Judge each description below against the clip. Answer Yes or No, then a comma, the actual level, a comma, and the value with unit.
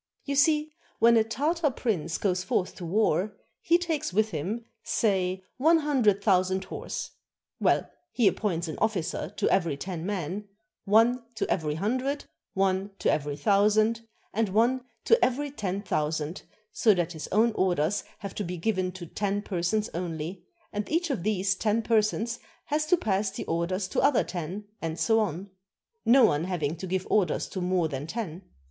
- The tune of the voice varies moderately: Yes, average, 4.2 semitones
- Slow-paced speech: No, average, 170 wpm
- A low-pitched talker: No, high, 200 Hz